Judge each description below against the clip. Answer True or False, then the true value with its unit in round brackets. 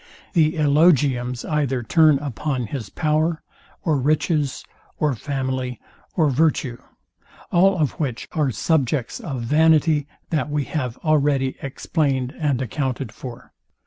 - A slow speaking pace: True (120 wpm)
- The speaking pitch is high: False (145 Hz)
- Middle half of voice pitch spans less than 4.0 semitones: True (3.1 semitones)